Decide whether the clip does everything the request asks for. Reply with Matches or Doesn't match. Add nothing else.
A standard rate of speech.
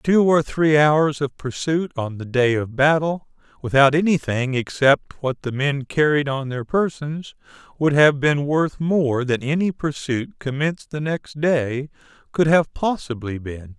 Matches